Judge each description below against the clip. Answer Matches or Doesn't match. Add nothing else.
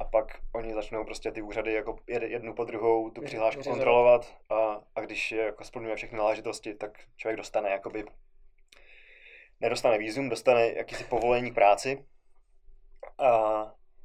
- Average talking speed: Matches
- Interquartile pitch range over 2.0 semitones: Matches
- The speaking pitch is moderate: Doesn't match